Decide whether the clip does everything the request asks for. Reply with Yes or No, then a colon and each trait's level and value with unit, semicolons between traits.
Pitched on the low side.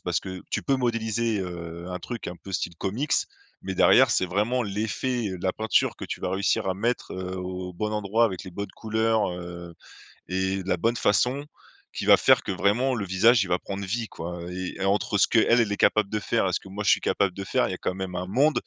Yes: low, 100 Hz